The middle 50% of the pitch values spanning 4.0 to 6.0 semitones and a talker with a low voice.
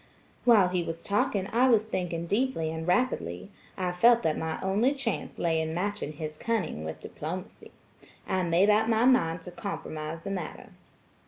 No: average, 5.3 semitones; medium, 180 Hz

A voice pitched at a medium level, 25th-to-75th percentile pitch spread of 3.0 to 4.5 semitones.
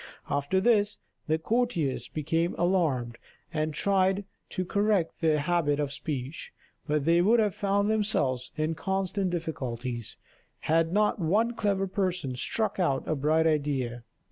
No: medium, 165 Hz; average, 5.1 semitones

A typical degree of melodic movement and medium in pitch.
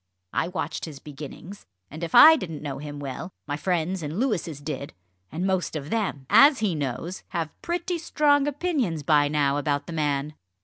No: wide, 6.2 semitones; medium, 165 Hz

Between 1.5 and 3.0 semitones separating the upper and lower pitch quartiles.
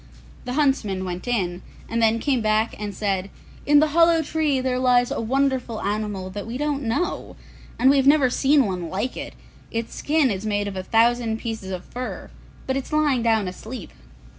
No: average, 4.8 semitones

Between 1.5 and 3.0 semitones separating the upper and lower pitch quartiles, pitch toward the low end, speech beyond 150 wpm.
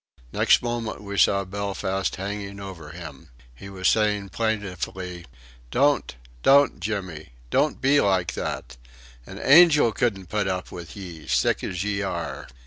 No: average, 2.7 semitones; low, 100 Hz; average, 140 wpm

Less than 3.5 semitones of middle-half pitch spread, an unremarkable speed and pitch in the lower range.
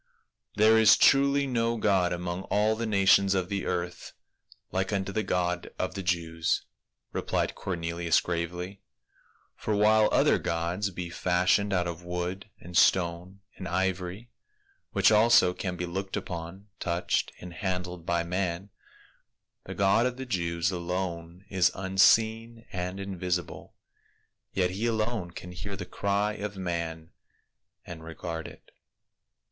Yes: average, 2.8 semitones; average, 145 wpm; very low, 95 Hz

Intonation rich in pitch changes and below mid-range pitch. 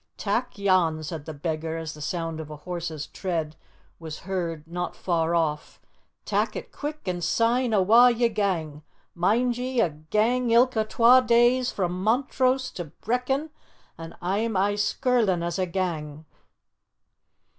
No: wide, 6.3 semitones; medium, 185 Hz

